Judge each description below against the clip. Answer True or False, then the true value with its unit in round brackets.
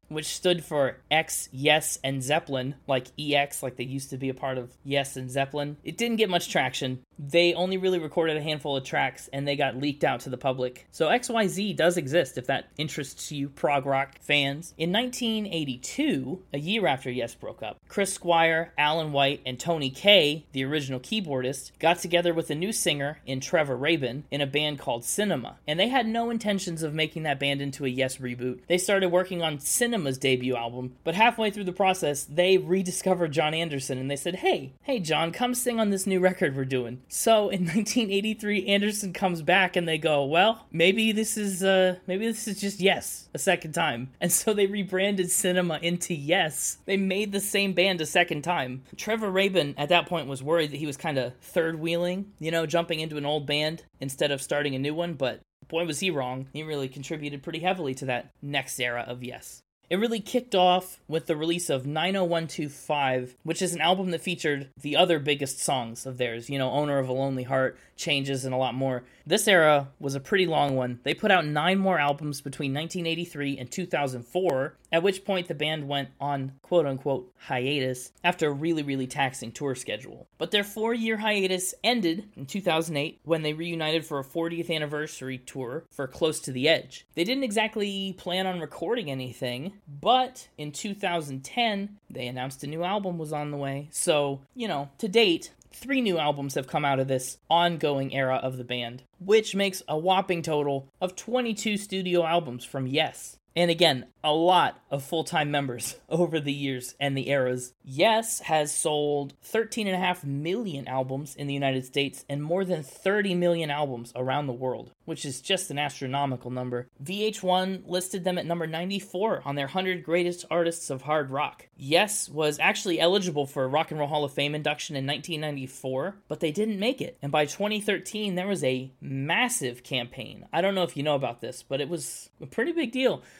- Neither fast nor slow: True (195 wpm)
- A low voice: False (155 Hz)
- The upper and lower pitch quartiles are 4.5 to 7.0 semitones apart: True (5.1 semitones)